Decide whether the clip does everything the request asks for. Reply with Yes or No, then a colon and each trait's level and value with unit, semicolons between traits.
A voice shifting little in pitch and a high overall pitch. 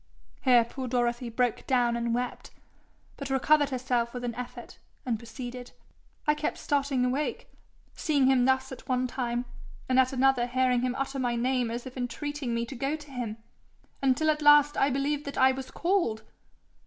Yes: narrow, 2.1 semitones; very high, 255 Hz